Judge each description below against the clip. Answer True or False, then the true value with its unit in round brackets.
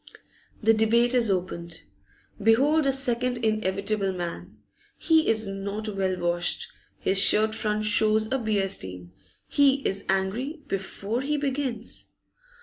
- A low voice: False (215 Hz)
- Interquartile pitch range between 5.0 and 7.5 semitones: False (4.1 semitones)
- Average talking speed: False (130 wpm)